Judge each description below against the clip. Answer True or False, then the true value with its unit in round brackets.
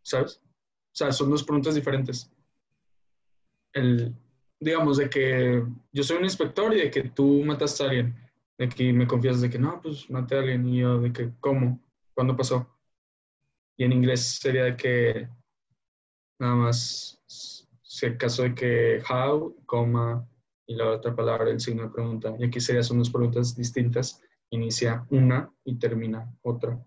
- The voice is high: False (125 Hz)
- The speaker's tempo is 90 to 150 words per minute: False (165 wpm)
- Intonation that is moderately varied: False (1.9 semitones)